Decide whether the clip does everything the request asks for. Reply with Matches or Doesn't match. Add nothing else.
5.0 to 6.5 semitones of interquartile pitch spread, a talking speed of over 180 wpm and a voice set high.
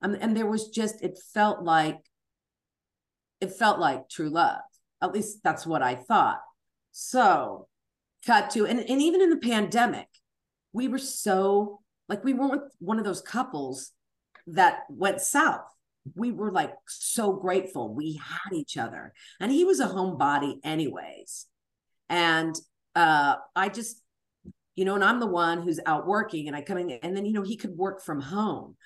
Doesn't match